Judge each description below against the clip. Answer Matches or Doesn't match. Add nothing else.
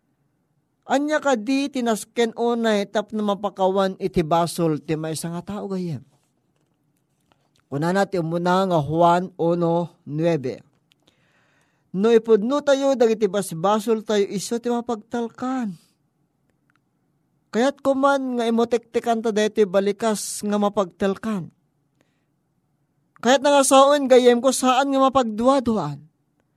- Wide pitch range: Matches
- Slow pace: Matches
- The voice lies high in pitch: Matches